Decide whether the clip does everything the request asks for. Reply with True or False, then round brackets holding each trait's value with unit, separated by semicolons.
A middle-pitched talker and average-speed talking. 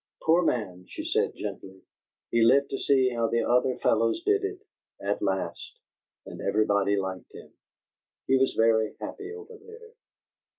False (125 Hz; 155 wpm)